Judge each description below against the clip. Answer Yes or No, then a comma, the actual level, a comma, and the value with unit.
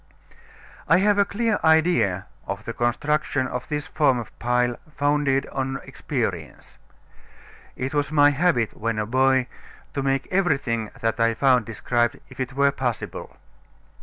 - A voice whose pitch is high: No, low, 135 Hz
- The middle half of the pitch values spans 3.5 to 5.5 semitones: Yes, average, 3.8 semitones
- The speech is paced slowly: No, average, 145 wpm